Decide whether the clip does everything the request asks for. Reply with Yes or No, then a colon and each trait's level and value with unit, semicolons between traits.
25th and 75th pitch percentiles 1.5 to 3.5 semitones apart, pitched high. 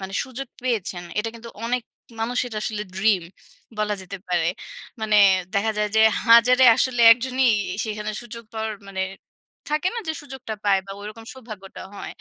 Yes: average, 3.2 semitones; high, 220 Hz